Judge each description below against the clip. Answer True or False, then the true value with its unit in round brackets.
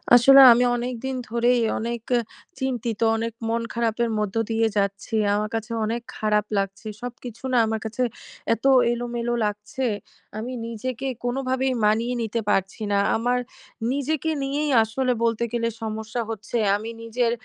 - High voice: True (235 Hz)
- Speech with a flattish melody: True (2.1 semitones)